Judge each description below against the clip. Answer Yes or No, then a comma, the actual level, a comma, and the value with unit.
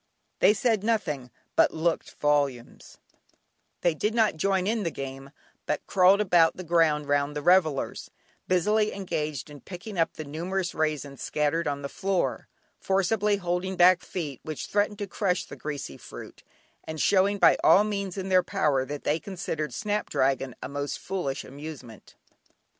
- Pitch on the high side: No, medium, 170 Hz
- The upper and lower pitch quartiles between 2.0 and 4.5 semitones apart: No, average, 4.9 semitones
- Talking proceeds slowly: No, average, 160 wpm